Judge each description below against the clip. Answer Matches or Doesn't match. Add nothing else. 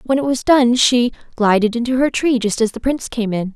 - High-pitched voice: Matches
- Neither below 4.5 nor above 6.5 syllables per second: Matches